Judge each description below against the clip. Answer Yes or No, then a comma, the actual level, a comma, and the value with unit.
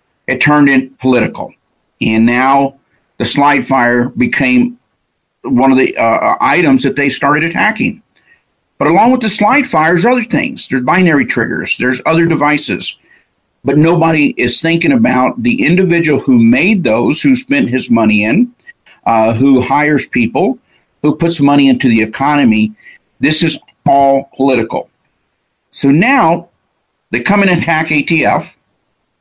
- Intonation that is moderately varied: No, wide, 7.6 semitones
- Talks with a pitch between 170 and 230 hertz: No, medium, 150 Hz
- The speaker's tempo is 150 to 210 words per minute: No, average, 140 wpm